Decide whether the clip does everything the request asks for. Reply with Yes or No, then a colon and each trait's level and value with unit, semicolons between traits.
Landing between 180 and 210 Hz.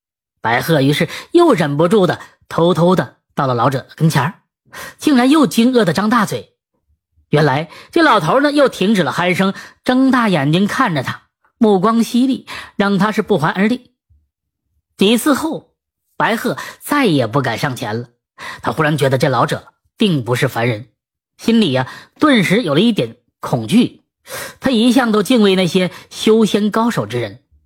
Yes: medium, 185 Hz